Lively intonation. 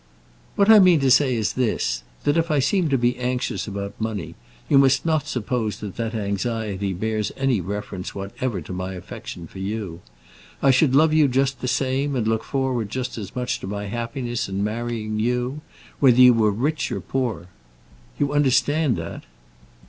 No: average, 4.5 semitones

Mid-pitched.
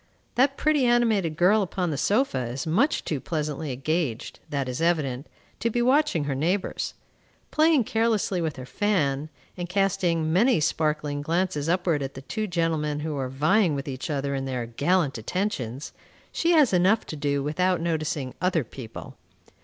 Yes: medium, 160 Hz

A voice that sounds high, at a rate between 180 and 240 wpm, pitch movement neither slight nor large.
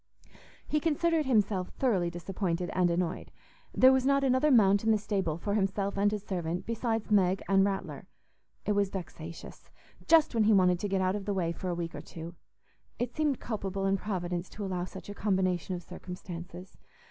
Yes: high, 195 Hz; average, 190 wpm; average, 3.3 semitones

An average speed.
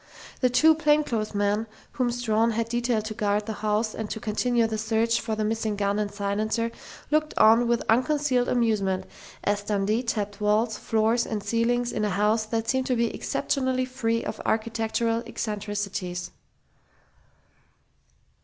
Yes: average, 150 wpm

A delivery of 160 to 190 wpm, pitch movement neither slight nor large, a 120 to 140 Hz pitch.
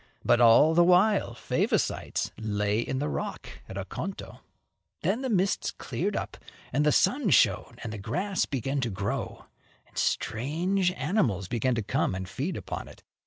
No: average, 165 wpm; wide, 8.9 semitones; low, 135 Hz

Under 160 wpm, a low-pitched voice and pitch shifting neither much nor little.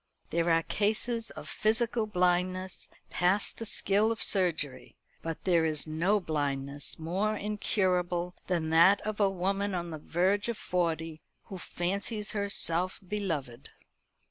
No: slow, 135 wpm; medium, 180 Hz; average, 3.8 semitones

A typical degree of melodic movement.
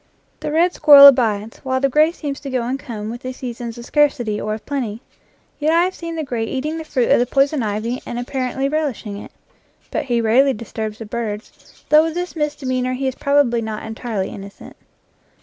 Yes: average, 4.2 semitones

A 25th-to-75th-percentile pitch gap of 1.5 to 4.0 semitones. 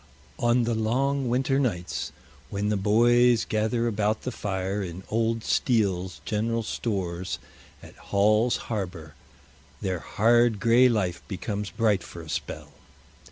Yes: average, 3.5 semitones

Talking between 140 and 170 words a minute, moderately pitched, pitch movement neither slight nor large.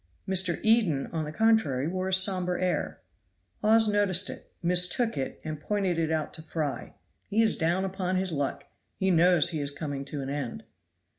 No: average, 180 wpm; medium, 180 Hz; average, 3.8 semitones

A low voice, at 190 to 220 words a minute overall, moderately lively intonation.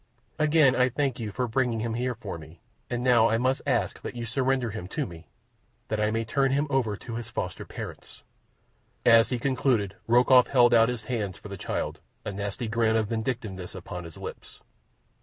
Yes: low, 115 Hz; average, 195 wpm; average, 3.1 semitones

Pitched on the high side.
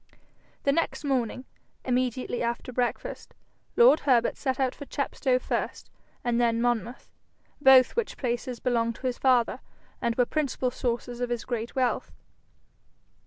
Yes: very high, 250 Hz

